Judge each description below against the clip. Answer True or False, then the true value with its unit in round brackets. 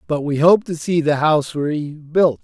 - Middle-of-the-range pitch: True (155 Hz)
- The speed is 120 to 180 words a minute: False (200 wpm)